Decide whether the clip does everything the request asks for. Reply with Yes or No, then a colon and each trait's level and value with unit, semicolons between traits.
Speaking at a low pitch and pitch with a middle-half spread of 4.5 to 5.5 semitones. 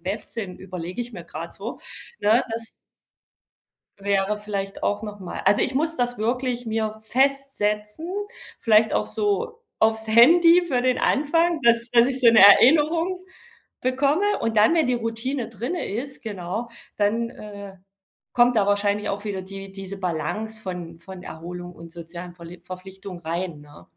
No: high, 215 Hz; average, 4.8 semitones